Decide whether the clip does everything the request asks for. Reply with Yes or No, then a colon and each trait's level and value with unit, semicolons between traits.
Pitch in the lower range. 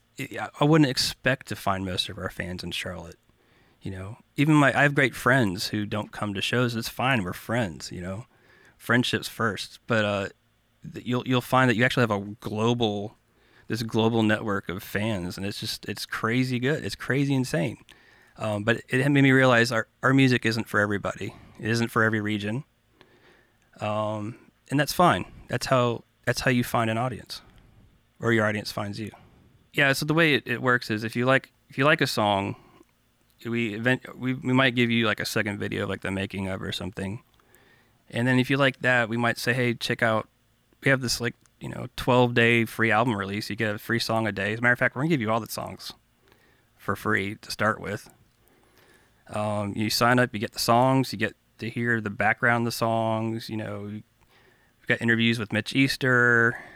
Yes: low, 115 Hz